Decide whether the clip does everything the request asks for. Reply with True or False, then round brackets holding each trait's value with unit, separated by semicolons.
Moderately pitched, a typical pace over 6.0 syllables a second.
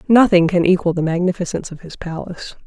True (180 Hz; 6.6 syllables/s)